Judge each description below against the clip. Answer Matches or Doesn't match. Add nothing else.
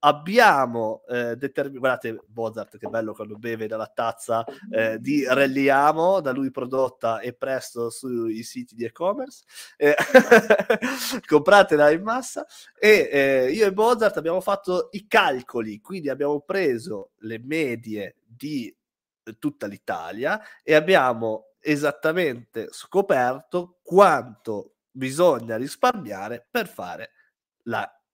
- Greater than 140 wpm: Doesn't match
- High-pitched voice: Doesn't match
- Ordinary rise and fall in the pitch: Doesn't match